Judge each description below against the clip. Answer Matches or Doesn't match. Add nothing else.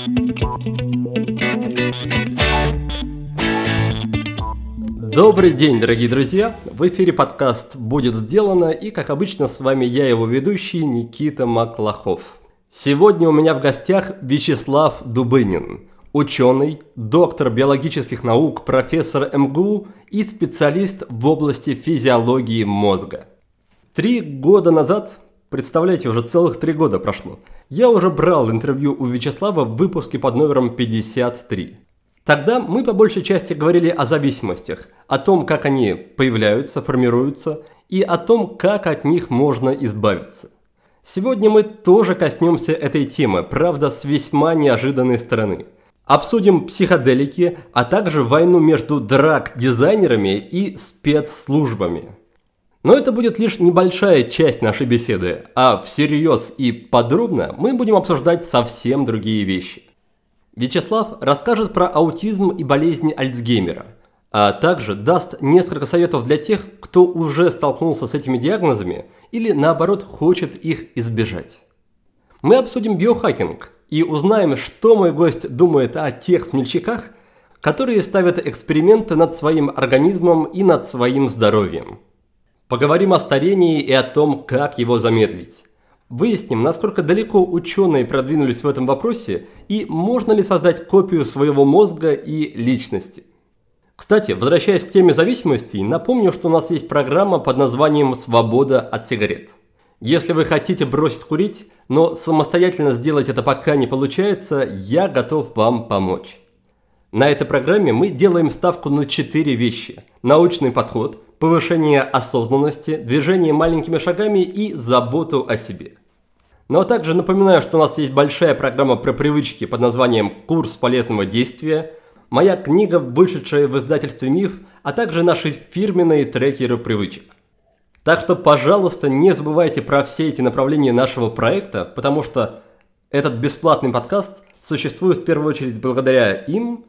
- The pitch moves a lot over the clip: Matches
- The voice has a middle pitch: Matches